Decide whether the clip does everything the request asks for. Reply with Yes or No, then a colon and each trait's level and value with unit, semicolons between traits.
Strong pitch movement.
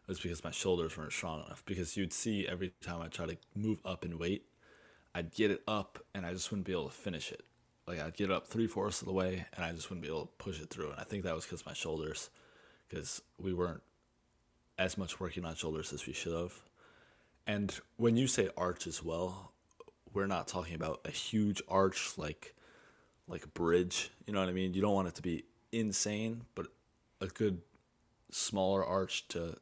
No: average, 3.1 semitones